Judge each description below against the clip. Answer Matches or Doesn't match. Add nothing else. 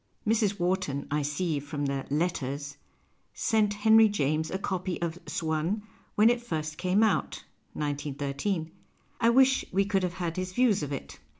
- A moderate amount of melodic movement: Doesn't match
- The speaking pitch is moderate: Matches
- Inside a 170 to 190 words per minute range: Matches